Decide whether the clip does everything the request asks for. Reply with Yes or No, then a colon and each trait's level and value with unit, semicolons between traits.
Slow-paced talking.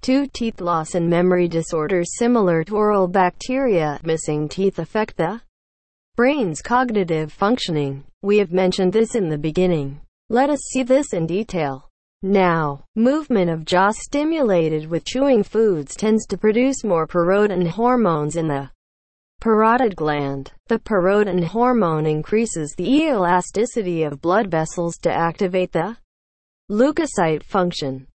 Yes: slow, 130 wpm